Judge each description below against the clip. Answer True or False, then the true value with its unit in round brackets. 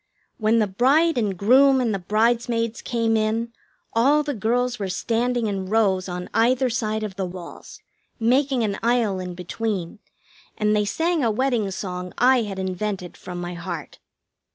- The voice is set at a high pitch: True (220 Hz)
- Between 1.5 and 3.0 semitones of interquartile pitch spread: False (4.1 semitones)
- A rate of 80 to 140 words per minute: False (165 wpm)